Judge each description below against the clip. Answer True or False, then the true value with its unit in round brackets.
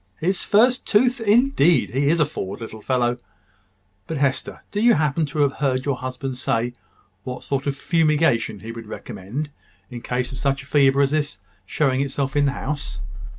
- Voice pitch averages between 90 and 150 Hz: True (140 Hz)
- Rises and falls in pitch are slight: False (3.4 semitones)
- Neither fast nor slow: True (185 wpm)